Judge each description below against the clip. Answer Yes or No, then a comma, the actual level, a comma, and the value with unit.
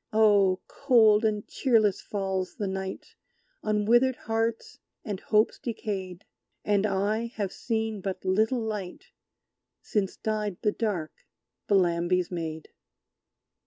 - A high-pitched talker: Yes, high, 210 Hz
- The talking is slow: Yes, slow, 115 wpm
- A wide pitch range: No, narrow, 2.6 semitones